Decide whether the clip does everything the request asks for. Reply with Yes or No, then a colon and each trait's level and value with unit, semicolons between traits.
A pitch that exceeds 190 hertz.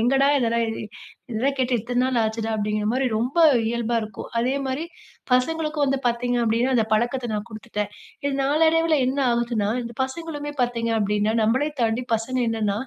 Yes: high, 240 Hz